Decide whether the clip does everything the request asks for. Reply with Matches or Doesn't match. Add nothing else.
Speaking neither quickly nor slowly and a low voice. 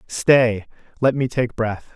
Matches